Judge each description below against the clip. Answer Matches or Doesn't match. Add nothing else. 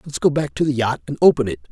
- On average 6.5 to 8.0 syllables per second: Matches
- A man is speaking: Matches